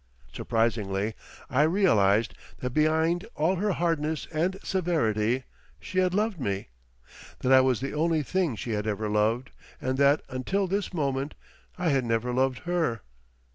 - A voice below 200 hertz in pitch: Yes, medium, 140 Hz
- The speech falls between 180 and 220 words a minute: No, average, 150 wpm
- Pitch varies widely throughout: Yes, wide, 6.9 semitones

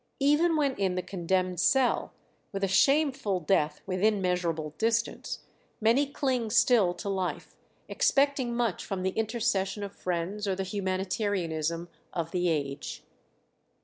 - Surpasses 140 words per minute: No, slow, 135 wpm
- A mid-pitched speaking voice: No, high, 195 Hz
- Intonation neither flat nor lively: Yes, average, 4.8 semitones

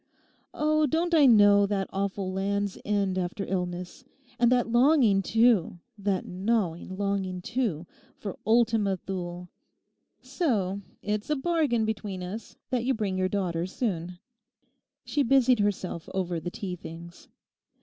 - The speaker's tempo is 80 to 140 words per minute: Yes, slow, 135 wpm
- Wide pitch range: No, average, 4.1 semitones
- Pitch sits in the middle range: No, high, 200 Hz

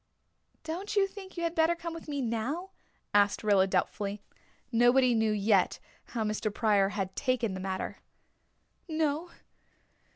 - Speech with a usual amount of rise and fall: No, wide, 8.0 semitones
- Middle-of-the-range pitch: No, high, 235 Hz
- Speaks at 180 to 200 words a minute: No, average, 140 wpm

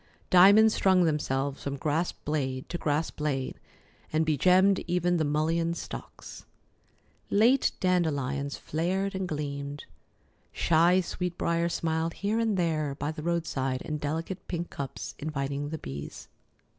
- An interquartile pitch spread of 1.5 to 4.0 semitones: Yes, average, 3.7 semitones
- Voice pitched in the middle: Yes, medium, 160 Hz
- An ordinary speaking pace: No, slow, 130 wpm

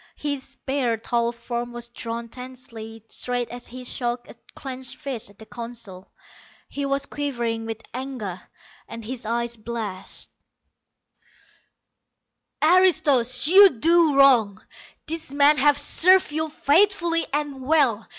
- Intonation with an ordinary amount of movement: Yes, average, 3.7 semitones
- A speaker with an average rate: No, slow, 125 wpm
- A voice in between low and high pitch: No, very high, 250 Hz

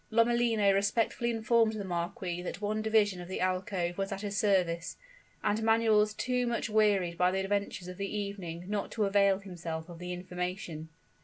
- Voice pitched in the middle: No, high, 200 Hz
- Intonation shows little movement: No, average, 3.2 semitones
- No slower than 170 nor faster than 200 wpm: Yes, average, 180 wpm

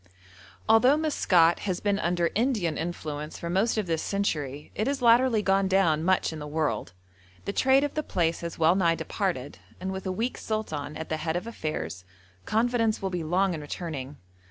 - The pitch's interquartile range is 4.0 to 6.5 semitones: Yes, average, 5.3 semitones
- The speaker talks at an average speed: Yes, average, 190 wpm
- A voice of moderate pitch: Yes, medium, 180 Hz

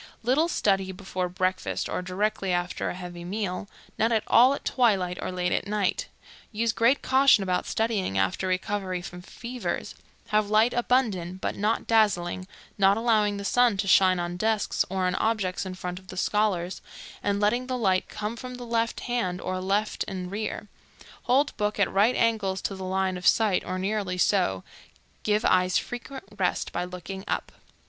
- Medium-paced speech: Yes, average, 180 wpm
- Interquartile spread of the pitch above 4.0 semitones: No, average, 3.3 semitones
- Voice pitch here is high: Yes, high, 200 Hz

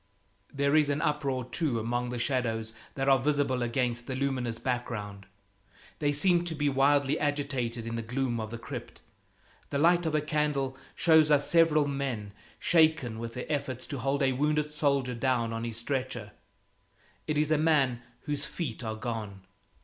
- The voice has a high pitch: No, low, 135 Hz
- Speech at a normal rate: Yes, average, 170 wpm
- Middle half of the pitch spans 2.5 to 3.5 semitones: No, average, 3.9 semitones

